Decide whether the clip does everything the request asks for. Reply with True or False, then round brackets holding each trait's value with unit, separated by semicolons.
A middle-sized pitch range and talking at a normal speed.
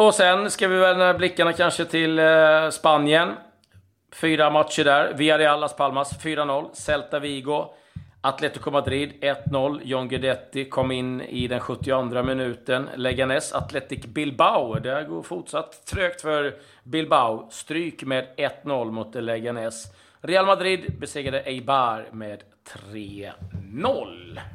False (3.8 semitones; 120 wpm)